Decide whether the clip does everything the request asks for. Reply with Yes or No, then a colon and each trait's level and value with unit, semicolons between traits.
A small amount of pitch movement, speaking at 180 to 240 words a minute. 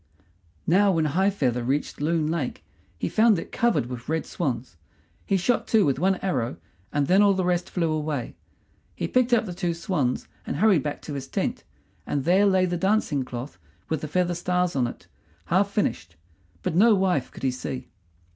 No: wide, 5.5 semitones; average, 195 wpm